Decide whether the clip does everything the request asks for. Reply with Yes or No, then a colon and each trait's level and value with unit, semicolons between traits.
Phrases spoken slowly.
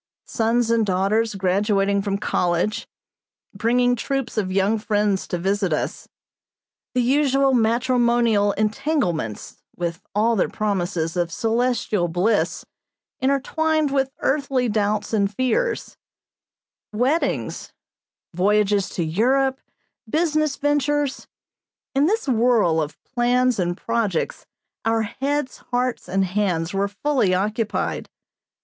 Yes: slow, 110 wpm